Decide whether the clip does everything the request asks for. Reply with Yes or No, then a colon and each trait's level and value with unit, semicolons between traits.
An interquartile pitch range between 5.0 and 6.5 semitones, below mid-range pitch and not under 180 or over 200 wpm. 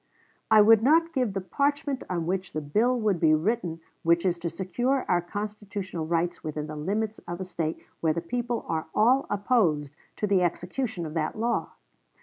No: average, 5.3 semitones; high, 190 Hz; average, 185 wpm